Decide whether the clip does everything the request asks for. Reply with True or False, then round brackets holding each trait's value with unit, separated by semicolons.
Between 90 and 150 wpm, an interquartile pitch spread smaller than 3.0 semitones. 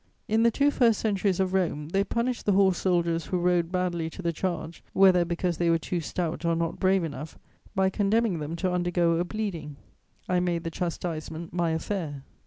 False (195 wpm; 2.5 semitones)